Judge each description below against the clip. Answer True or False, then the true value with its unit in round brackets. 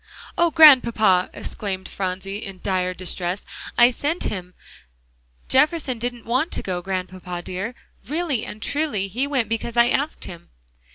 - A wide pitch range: True (6.0 semitones)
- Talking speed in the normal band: True (145 wpm)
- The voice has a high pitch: True (220 Hz)